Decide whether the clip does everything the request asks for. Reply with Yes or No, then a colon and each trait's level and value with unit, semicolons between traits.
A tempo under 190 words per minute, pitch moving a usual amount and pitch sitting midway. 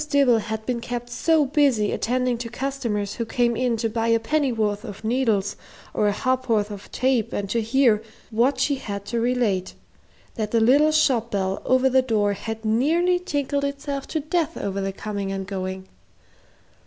No: average, 180 wpm; average, 4.1 semitones; high, 235 Hz